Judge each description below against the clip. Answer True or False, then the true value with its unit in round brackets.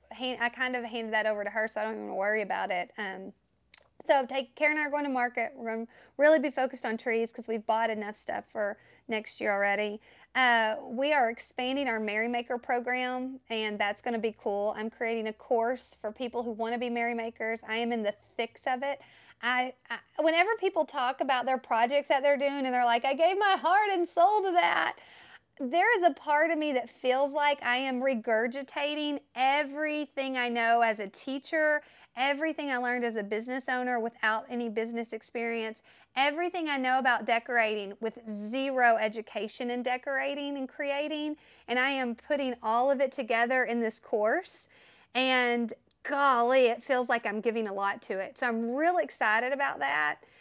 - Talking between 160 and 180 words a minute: False (195 wpm)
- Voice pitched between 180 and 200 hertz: False (245 Hz)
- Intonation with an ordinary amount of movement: True (3.6 semitones)